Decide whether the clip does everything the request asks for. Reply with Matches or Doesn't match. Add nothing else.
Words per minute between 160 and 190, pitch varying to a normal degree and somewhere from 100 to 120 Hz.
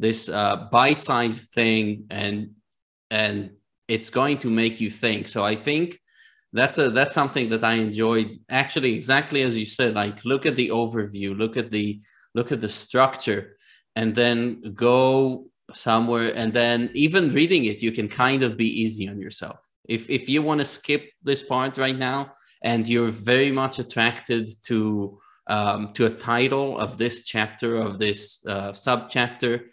Matches